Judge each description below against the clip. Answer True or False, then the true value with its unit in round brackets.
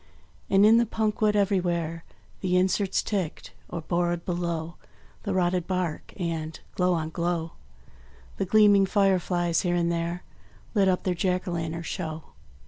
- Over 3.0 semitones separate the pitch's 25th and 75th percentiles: False (2.4 semitones)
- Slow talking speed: False (150 wpm)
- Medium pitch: True (180 Hz)